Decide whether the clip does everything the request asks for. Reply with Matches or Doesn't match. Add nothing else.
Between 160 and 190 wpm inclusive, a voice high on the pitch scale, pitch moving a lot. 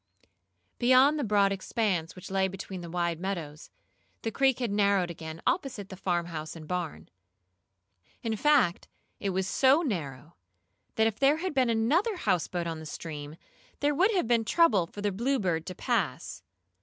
Matches